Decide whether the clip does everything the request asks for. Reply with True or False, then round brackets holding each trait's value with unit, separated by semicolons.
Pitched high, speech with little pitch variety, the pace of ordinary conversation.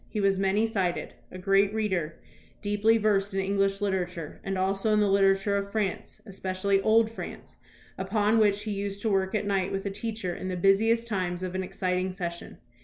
True (195 Hz; 1.7 semitones; 195 wpm)